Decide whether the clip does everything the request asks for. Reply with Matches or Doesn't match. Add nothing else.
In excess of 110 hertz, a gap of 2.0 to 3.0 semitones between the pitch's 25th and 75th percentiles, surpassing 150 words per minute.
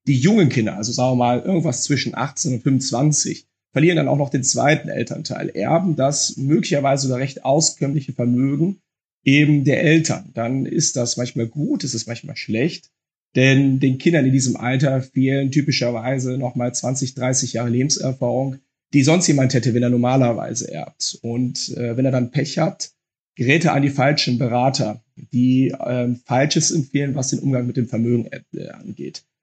Matches